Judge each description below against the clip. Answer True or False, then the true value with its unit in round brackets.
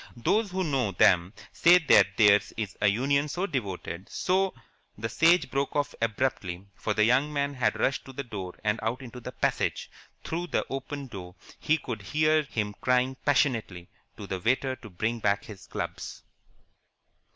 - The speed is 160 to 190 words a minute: True (175 wpm)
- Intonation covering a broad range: True (5.7 semitones)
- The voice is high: False (125 Hz)